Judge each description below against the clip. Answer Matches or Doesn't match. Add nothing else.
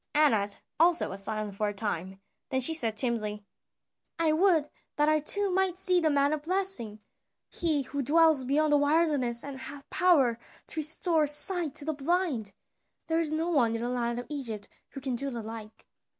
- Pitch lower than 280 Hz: Doesn't match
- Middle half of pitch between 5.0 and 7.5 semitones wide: Matches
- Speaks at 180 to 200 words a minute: Matches